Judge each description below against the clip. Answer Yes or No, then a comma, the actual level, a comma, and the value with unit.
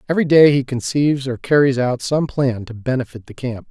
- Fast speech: Yes, fast, 210 wpm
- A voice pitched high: No, low, 130 Hz